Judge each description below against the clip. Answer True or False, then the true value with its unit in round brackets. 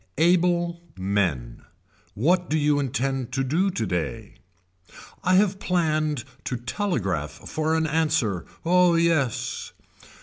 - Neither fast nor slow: False (110 wpm)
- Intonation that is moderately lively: False (6.8 semitones)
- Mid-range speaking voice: True (155 Hz)